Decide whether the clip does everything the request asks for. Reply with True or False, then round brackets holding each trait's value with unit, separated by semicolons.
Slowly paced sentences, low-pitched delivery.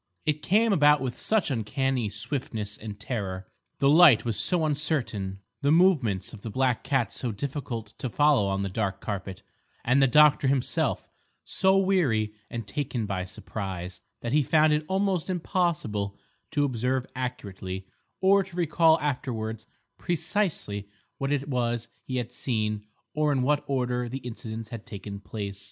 False (155 wpm; 125 Hz)